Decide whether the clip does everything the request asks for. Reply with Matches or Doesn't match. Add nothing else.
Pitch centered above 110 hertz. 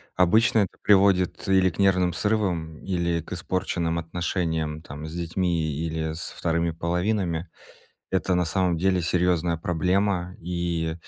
Doesn't match